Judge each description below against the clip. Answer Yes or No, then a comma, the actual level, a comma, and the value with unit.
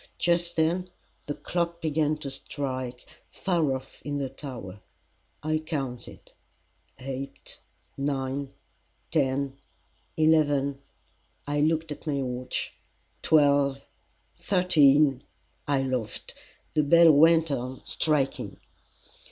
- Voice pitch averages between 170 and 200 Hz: No, medium, 145 Hz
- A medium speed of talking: No, slow, 100 wpm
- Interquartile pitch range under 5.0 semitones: Yes, average, 2.8 semitones